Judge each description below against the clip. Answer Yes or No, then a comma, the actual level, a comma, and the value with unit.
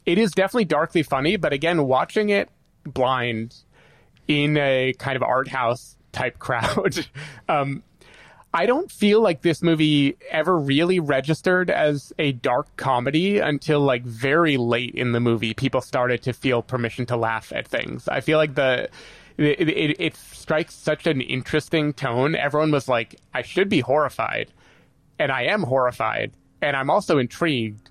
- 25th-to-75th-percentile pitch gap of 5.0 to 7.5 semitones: No, average, 3.9 semitones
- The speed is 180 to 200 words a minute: No, average, 160 wpm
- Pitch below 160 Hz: Yes, medium, 140 Hz